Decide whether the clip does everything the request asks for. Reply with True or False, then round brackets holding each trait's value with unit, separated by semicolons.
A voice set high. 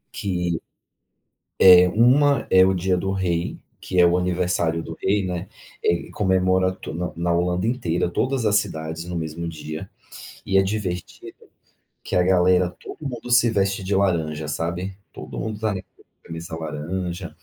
False (90 Hz)